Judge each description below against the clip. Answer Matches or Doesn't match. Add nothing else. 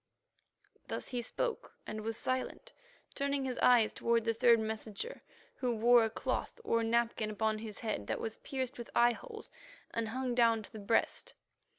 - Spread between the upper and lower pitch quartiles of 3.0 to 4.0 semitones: Doesn't match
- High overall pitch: Matches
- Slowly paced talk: Doesn't match